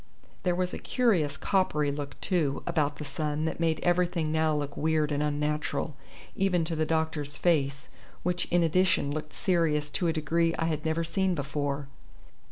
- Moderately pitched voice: Yes, medium, 160 Hz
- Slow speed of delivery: No, average, 175 wpm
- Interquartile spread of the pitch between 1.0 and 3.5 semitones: Yes, narrow, 2.6 semitones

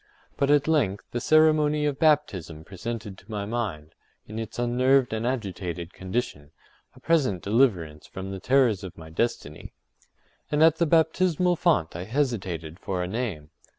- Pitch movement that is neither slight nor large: No, wide, 7.6 semitones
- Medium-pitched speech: No, low, 115 Hz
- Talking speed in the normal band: Yes, average, 155 wpm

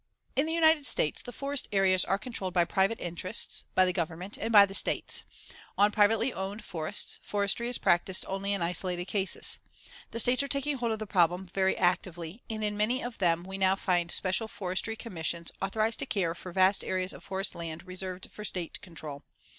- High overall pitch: Yes, high, 195 Hz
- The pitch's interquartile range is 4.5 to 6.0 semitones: No, average, 3.4 semitones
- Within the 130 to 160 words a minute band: No, average, 195 wpm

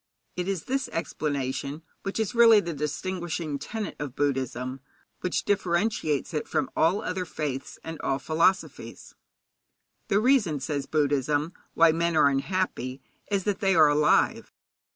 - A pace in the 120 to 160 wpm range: Yes, average, 140 wpm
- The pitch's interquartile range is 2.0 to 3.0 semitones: No, average, 4.8 semitones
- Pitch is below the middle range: No, medium, 160 Hz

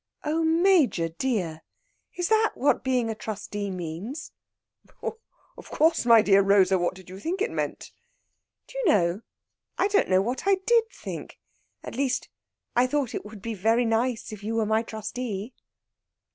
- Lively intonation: Yes, wide, 6.8 semitones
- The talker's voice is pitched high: Yes, high, 225 Hz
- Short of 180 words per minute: Yes, average, 165 wpm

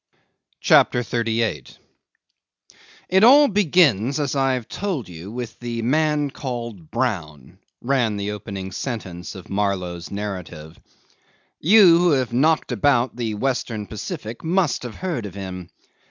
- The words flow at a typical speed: No, slow, 125 wpm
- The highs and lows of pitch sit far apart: Yes, wide, 6.1 semitones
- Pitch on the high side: No, low, 115 Hz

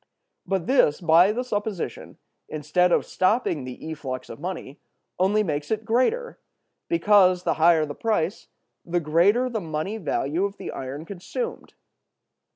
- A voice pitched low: No, medium, 180 Hz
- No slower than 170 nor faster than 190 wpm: No, average, 145 wpm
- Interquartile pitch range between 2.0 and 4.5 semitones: No, wide, 5.4 semitones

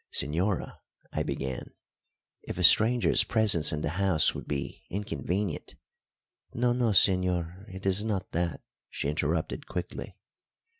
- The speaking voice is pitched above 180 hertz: No, very low, 90 Hz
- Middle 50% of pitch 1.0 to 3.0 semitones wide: No, average, 4.4 semitones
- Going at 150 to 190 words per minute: No, slow, 135 wpm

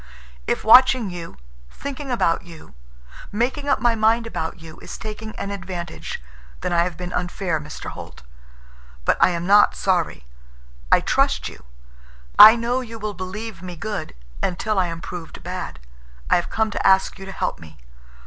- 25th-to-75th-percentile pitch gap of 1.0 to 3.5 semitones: No, average, 4.5 semitones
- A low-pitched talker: No, high, 190 Hz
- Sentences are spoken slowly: No, average, 170 wpm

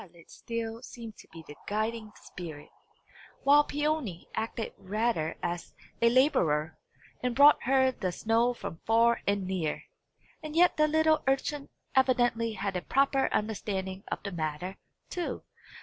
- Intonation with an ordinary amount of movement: No, wide, 6.0 semitones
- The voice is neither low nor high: No, high, 225 Hz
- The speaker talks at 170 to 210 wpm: No, average, 145 wpm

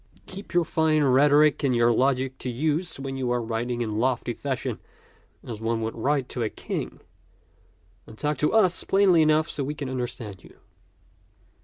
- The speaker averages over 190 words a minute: No, average, 175 wpm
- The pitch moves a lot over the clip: No, average, 4.1 semitones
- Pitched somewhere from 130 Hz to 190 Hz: Yes, low, 135 Hz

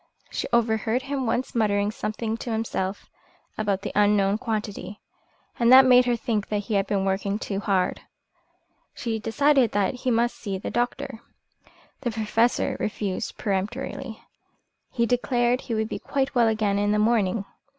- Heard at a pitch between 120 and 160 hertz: No, high, 220 Hz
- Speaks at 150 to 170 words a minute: Yes, average, 155 wpm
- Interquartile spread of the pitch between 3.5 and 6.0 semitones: No, average, 2.9 semitones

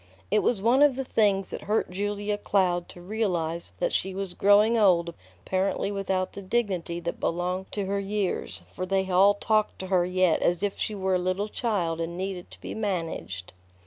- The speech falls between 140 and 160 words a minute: No, average, 195 wpm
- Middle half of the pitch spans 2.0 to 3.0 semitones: Yes, narrow, 2.4 semitones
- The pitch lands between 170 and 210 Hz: Yes, high, 190 Hz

